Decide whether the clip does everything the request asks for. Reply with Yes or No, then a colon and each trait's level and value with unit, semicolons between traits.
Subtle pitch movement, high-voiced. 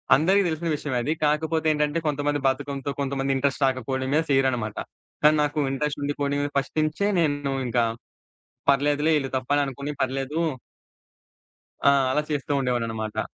No: narrow, 2.0 semitones; medium, 140 Hz